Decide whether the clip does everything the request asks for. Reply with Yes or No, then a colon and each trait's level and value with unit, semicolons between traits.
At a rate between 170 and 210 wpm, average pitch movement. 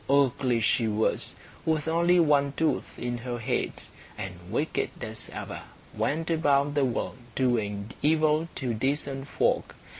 No: average, 140 wpm; average, 4.6 semitones